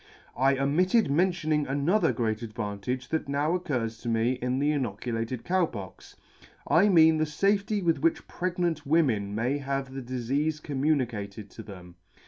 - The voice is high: No, medium, 140 Hz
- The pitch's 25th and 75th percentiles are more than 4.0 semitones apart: Yes, wide, 5.5 semitones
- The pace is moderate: Yes, average, 155 wpm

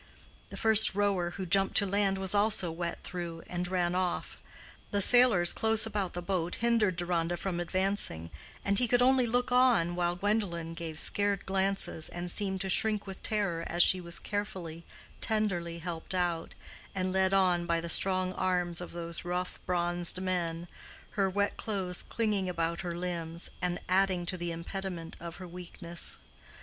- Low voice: No, medium, 180 Hz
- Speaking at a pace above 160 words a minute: Yes, average, 170 wpm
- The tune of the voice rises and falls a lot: No, narrow, 2.4 semitones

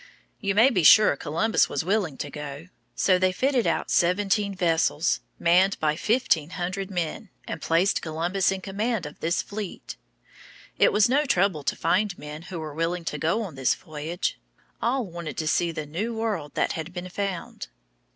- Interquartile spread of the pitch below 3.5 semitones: No, average, 4.1 semitones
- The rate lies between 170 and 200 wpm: Yes, average, 180 wpm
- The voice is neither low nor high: Yes, medium, 180 Hz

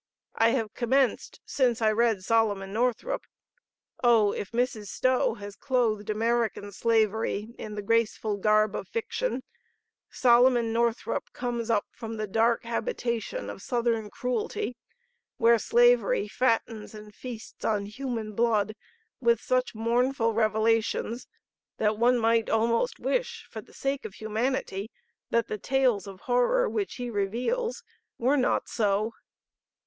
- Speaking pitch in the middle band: No, high, 230 Hz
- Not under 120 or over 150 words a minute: Yes, slow, 135 wpm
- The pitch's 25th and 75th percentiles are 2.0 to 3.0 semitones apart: Yes, narrow, 2.5 semitones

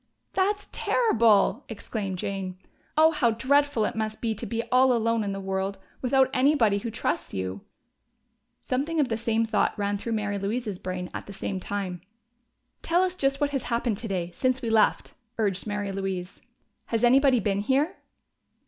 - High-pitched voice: Yes, high, 225 Hz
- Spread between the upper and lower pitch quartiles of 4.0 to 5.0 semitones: Yes, average, 4.7 semitones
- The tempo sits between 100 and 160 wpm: No, average, 170 wpm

